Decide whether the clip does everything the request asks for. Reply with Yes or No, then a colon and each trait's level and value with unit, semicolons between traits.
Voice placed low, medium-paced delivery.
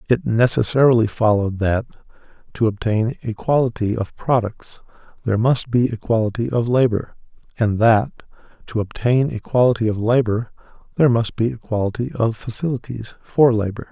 No: low, 115 Hz; slow, 130 wpm